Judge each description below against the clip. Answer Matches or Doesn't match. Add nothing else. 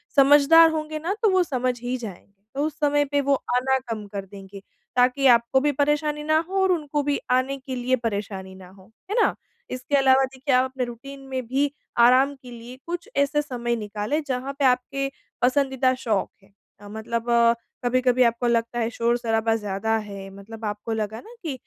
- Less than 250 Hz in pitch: Doesn't match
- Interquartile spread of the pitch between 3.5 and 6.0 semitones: Matches